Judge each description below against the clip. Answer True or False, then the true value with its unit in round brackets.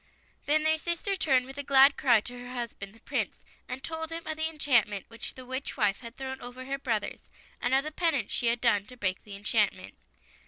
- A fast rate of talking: True (225 wpm)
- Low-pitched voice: False (255 Hz)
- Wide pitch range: False (3.8 semitones)